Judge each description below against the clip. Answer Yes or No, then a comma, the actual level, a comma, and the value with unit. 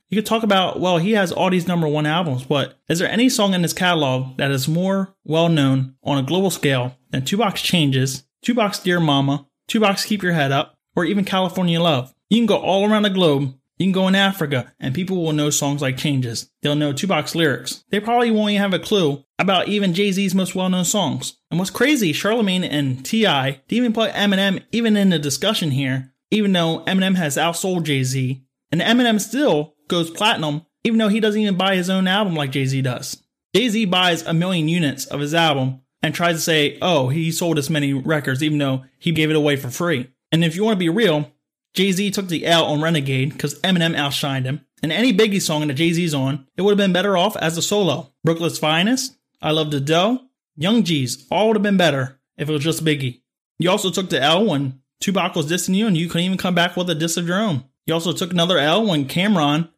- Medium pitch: Yes, medium, 165 Hz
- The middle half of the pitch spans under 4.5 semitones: No, average, 5.1 semitones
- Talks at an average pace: No, fast, 230 wpm